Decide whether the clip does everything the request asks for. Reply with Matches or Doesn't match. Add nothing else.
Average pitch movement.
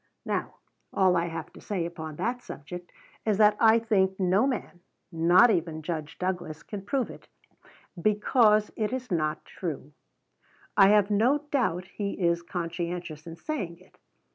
Matches